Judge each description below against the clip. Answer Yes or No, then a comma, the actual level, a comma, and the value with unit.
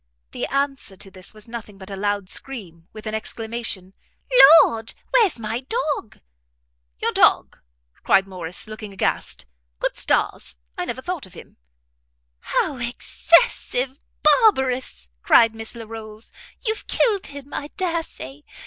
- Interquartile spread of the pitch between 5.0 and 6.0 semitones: Yes, wide, 5.6 semitones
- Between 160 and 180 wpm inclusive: No, slow, 135 wpm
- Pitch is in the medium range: No, high, 225 Hz